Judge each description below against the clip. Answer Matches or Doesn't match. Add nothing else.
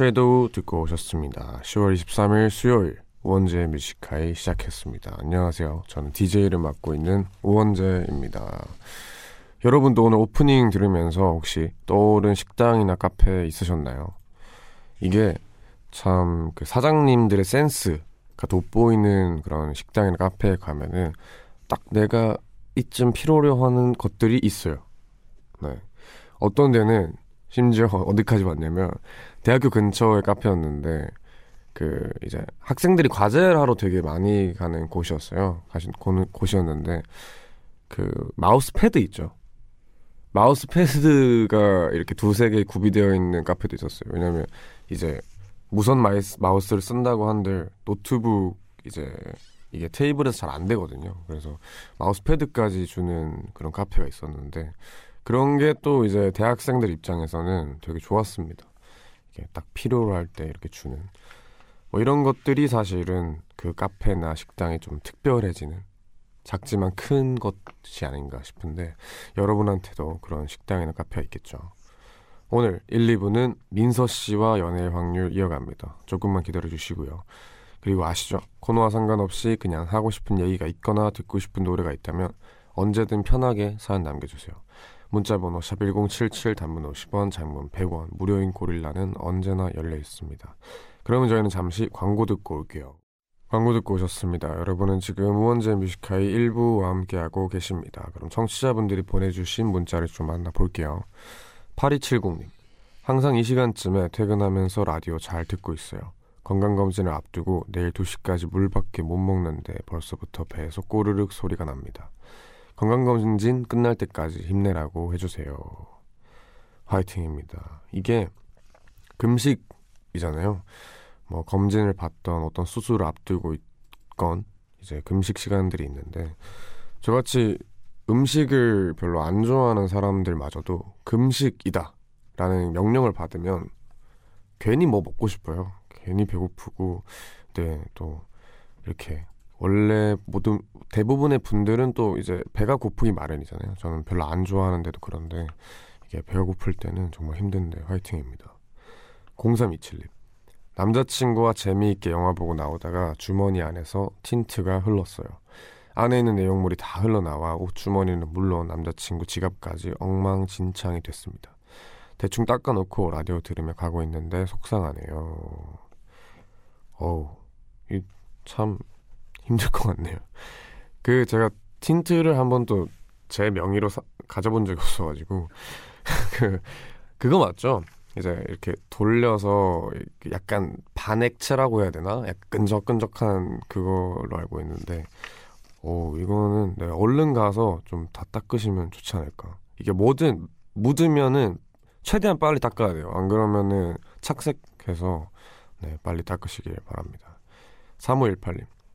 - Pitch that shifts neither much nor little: Matches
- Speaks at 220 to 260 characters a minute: Doesn't match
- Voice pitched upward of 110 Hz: Doesn't match